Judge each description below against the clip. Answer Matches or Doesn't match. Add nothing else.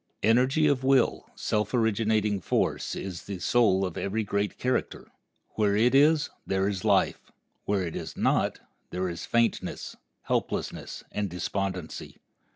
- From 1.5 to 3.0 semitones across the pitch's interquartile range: Doesn't match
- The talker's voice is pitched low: Matches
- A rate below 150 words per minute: Matches